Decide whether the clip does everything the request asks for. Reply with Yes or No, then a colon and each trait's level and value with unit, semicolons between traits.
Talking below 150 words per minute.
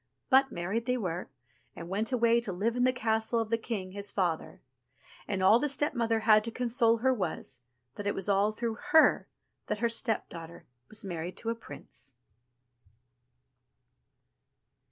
No: average, 165 wpm